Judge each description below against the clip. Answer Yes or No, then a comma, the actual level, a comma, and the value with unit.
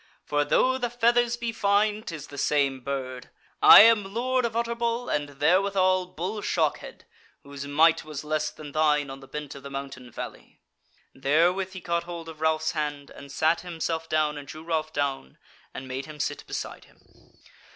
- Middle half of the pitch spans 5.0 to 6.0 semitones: Yes, wide, 5.4 semitones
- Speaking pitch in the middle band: Yes, medium, 155 Hz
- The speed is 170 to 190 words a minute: Yes, average, 180 wpm